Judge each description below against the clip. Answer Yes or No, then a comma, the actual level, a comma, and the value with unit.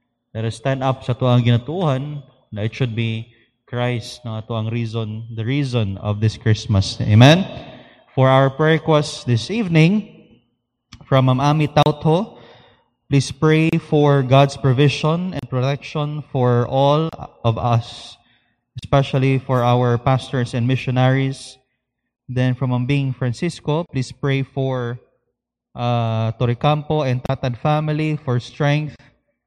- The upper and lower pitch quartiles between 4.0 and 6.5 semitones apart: No, average, 3.2 semitones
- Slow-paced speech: Yes, slow, 120 wpm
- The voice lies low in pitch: Yes, low, 130 Hz